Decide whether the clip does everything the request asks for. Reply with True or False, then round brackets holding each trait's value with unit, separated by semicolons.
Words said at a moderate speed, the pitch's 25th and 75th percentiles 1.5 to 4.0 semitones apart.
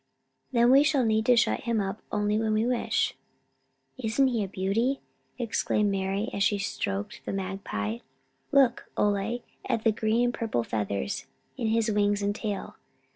True (165 wpm; 2.9 semitones)